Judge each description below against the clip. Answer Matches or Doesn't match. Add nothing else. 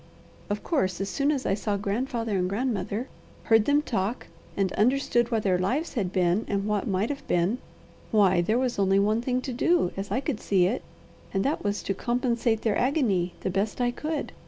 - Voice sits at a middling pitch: Doesn't match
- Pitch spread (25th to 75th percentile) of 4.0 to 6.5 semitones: Matches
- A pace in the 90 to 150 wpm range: Doesn't match